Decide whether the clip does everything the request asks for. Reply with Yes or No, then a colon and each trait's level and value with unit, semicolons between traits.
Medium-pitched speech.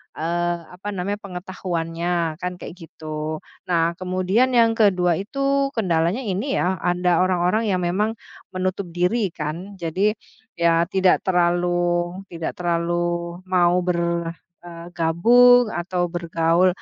Yes: medium, 180 Hz